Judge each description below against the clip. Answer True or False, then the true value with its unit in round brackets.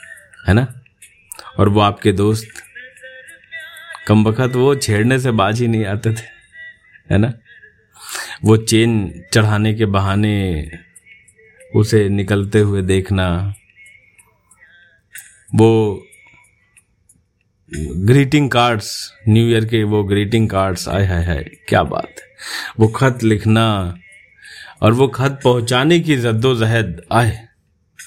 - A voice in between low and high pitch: False (110 Hz)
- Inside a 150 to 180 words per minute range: False (110 wpm)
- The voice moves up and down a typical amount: True (3.5 semitones)